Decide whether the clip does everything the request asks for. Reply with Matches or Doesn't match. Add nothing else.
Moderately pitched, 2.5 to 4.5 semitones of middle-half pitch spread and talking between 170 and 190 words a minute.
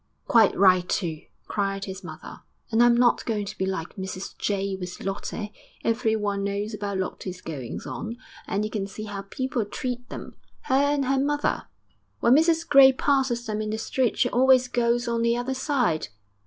Doesn't match